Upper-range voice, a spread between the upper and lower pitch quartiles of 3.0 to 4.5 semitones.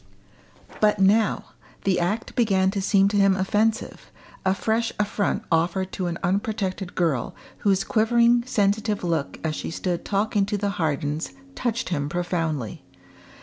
Yes: high, 195 Hz; average, 3.4 semitones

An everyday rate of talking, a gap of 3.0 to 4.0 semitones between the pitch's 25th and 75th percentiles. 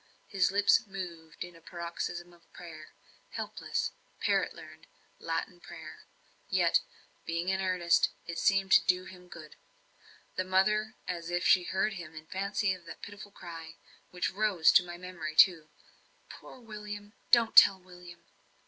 No: average, 145 wpm; narrow, 2.4 semitones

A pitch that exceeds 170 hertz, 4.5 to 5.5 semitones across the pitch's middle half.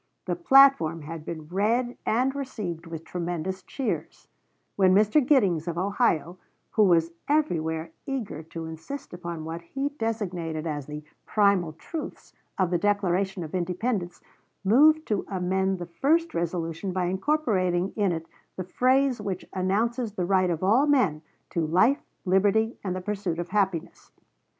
Yes: medium, 185 Hz; average, 4.8 semitones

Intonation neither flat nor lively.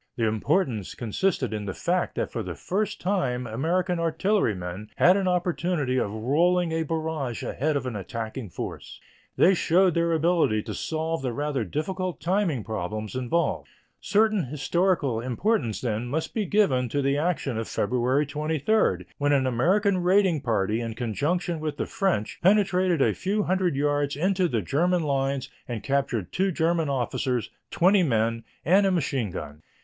No: wide, 6.9 semitones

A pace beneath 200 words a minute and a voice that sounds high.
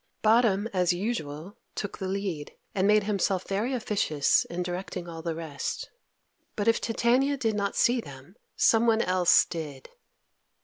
Yes: average, 145 wpm; high, 195 Hz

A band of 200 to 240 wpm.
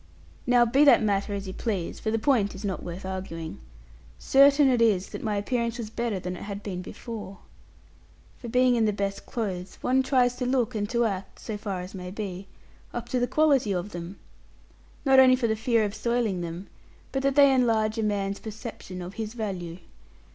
Yes: fast, 205 wpm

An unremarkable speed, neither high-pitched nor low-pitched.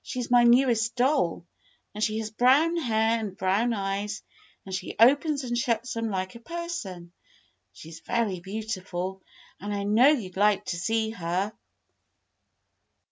No: average, 155 wpm; high, 220 Hz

